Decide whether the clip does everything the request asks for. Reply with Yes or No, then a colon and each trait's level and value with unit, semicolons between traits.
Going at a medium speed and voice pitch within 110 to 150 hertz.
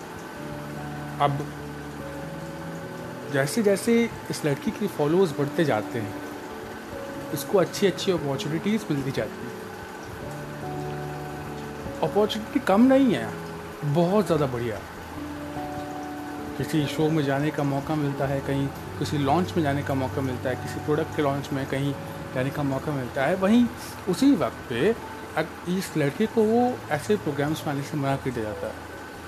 Yes: average, 145 wpm; medium, 140 Hz